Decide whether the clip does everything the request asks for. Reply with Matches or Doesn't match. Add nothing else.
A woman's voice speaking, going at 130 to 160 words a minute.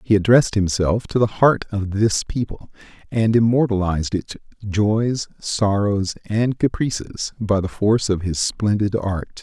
Doesn't match